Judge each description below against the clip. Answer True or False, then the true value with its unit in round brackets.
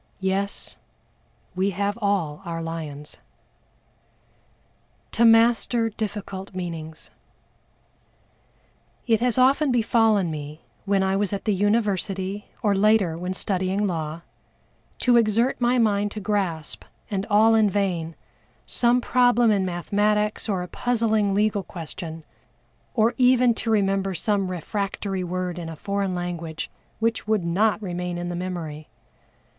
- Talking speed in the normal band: False (130 wpm)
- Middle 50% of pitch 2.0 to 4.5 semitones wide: True (3.5 semitones)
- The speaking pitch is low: False (200 Hz)